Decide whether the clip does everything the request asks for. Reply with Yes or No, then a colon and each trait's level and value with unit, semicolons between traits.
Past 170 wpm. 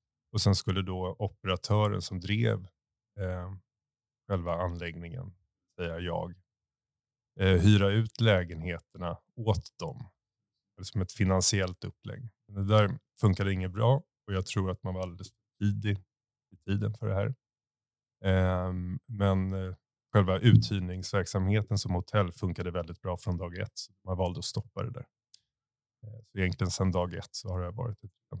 No: average, 155 wpm